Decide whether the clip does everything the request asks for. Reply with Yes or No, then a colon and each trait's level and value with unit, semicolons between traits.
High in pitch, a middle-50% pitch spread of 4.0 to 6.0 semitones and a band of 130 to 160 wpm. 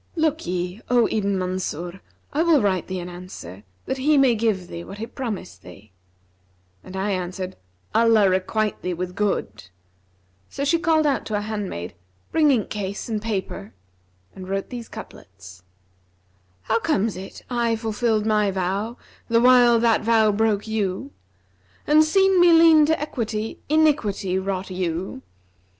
Yes: high, 210 Hz; average, 4.6 semitones; average, 150 wpm